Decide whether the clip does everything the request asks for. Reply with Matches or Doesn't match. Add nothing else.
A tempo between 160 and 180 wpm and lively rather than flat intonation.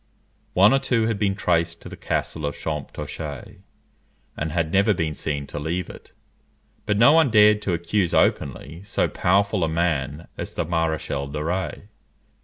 Doesn't match